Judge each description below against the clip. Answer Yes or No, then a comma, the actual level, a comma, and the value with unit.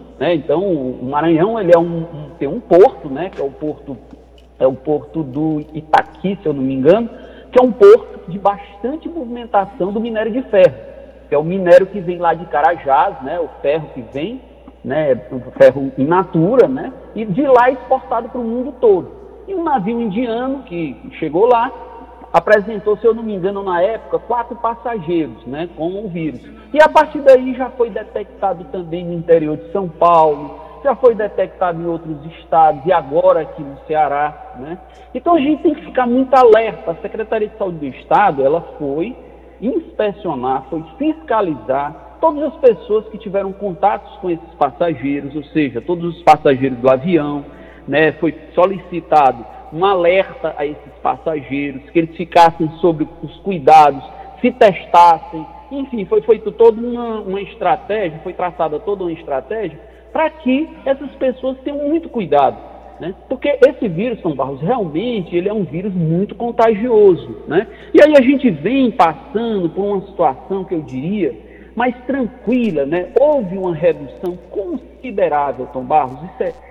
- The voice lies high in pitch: Yes, high, 195 Hz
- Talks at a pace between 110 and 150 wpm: No, average, 170 wpm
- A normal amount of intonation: No, wide, 7.4 semitones